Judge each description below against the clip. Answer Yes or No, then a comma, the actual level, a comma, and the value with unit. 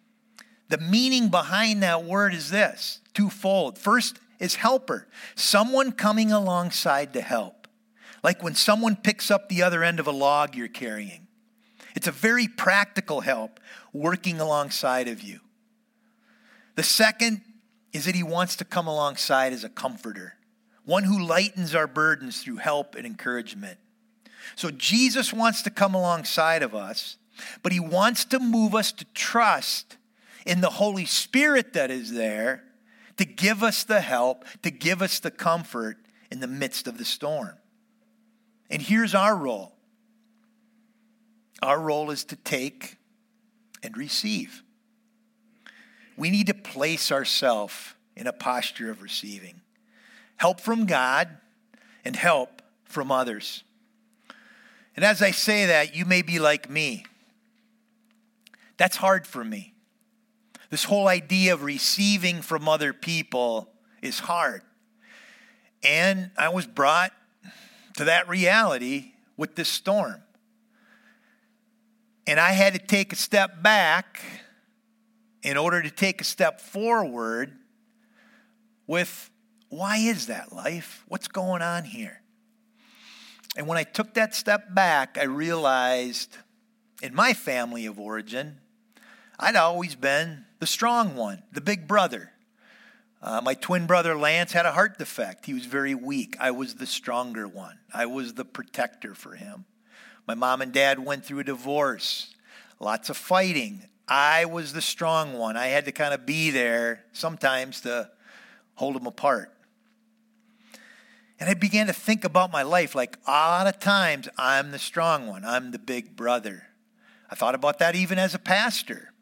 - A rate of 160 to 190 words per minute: No, average, 145 wpm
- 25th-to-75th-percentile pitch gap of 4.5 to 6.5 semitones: Yes, average, 5.3 semitones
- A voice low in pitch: No, high, 205 Hz